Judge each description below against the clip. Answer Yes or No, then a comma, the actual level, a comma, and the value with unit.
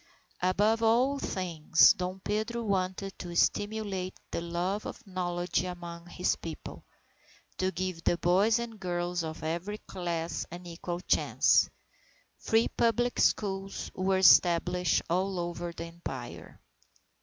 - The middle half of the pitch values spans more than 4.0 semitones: No, narrow, 2.5 semitones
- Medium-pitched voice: Yes, medium, 180 Hz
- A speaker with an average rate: No, slow, 125 wpm